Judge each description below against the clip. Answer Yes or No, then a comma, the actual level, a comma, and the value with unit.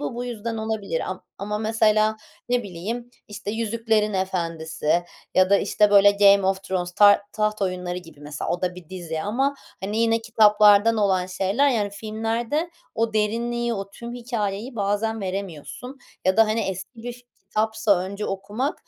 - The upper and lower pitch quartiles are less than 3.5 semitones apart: Yes, average, 3.1 semitones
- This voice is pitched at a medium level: No, high, 210 Hz